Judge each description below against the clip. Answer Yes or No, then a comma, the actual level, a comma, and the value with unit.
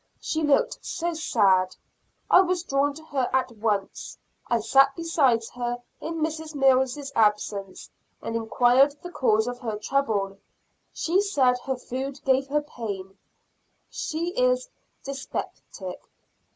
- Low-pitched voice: No, very high, 265 Hz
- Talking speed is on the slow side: Yes, slow, 130 wpm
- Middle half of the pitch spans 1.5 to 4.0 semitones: No, average, 5.3 semitones